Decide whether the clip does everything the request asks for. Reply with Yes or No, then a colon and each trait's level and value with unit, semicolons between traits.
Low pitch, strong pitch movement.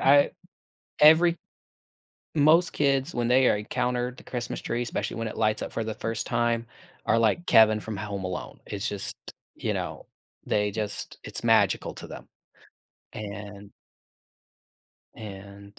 No: low, 115 Hz; average, 3.4 semitones